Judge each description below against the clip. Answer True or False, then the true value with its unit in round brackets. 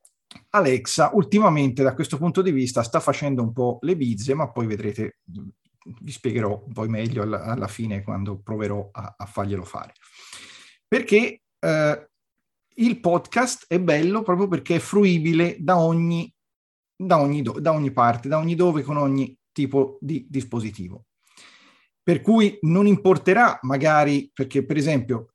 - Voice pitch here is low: False (145 Hz)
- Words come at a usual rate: True (150 wpm)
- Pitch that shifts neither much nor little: False (6.6 semitones)